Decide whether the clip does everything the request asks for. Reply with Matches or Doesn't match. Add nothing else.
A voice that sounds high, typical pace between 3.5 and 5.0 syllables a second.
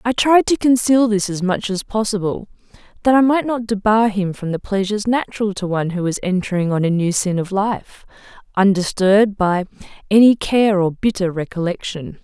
Doesn't match